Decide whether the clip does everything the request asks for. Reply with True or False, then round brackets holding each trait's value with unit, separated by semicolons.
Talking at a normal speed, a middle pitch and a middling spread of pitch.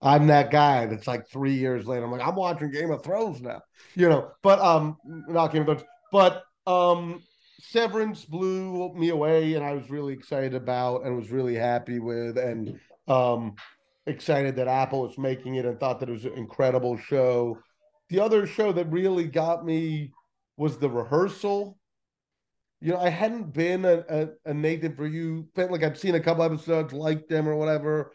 True (190 wpm; 155 Hz; 4.9 semitones)